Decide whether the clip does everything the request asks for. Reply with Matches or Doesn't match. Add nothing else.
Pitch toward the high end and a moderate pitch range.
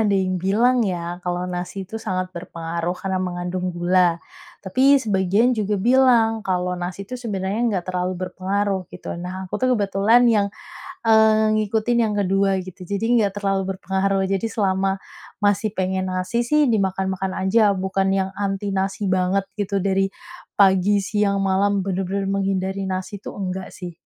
Doesn't match